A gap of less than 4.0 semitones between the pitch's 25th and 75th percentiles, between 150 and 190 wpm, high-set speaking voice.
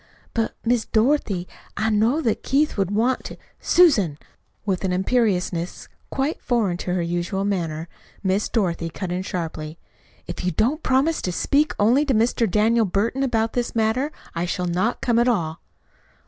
No: average, 5.3 semitones; average, 165 wpm; high, 215 Hz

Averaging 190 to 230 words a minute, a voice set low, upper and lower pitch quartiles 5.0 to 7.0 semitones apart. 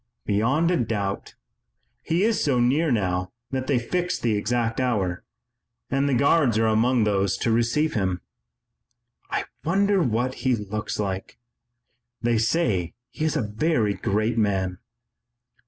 No: average, 140 wpm; low, 115 Hz; average, 5.3 semitones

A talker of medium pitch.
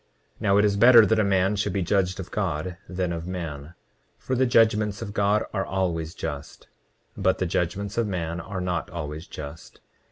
No: very low, 95 Hz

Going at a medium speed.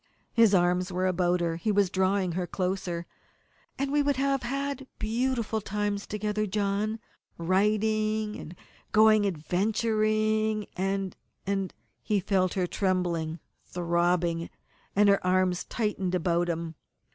No: slow, 130 wpm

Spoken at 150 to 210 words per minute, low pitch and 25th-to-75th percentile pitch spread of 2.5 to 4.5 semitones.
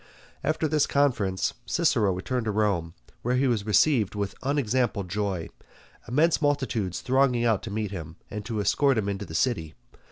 No: average, 165 wpm; low, 110 Hz; average, 4.9 semitones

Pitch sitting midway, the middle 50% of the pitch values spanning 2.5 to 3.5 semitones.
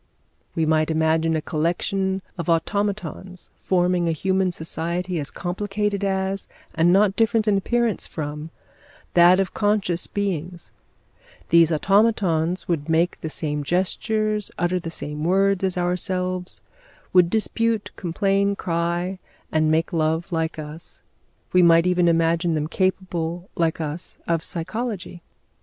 Yes: medium, 175 Hz; average, 3.0 semitones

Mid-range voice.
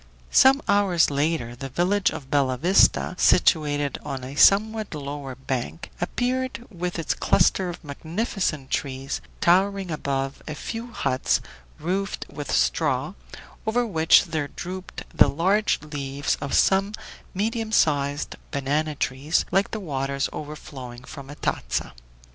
Yes: medium, 155 Hz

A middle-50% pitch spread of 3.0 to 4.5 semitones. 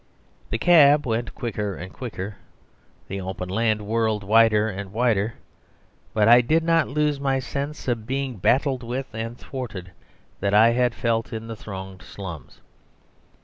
Yes: average, 4.0 semitones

